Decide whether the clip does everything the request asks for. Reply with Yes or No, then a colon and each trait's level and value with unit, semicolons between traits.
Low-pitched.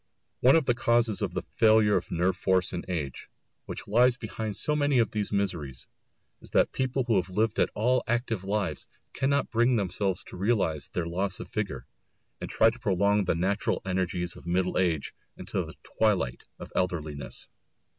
Yes: low, 100 Hz